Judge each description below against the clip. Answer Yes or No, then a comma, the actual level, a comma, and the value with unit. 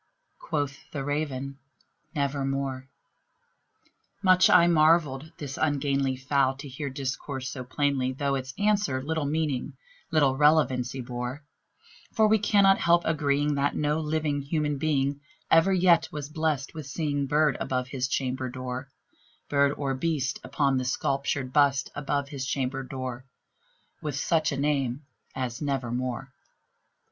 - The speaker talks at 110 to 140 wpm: Yes, slow, 135 wpm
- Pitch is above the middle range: No, medium, 140 Hz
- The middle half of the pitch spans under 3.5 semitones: Yes, narrow, 2.4 semitones